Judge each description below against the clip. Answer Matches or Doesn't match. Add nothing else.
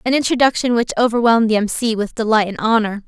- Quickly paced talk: Matches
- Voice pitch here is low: Doesn't match